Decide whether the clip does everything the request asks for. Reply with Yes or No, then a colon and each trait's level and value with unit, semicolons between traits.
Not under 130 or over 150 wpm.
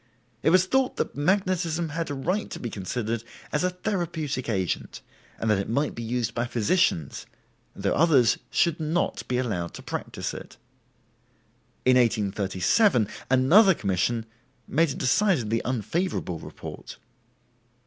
Yes: average, 140 wpm